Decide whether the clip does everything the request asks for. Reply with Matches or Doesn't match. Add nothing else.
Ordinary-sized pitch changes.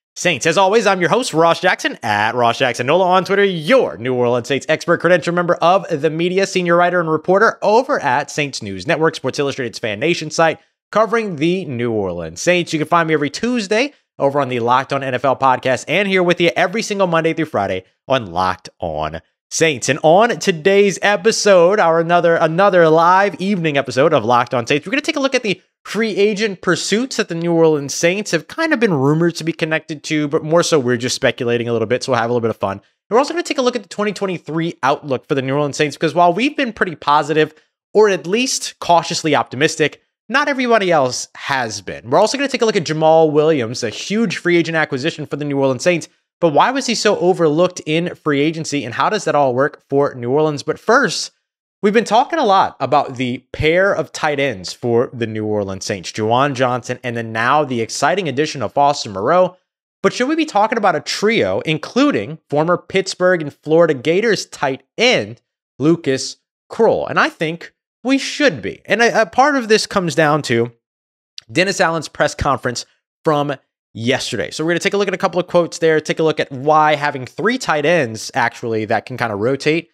Doesn't match